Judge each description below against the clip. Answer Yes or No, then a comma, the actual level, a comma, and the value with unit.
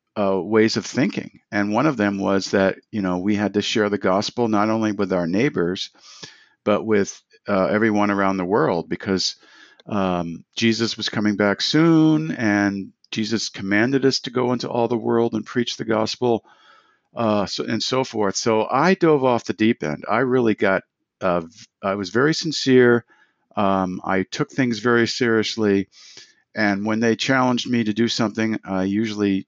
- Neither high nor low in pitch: No, low, 110 Hz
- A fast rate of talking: No, average, 180 wpm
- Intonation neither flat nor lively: Yes, average, 3.0 semitones